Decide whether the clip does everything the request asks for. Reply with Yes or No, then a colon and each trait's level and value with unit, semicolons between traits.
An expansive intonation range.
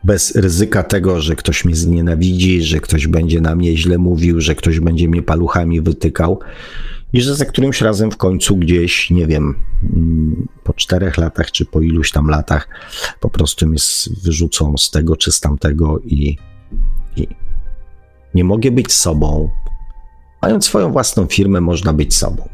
No: average, 2.9 semitones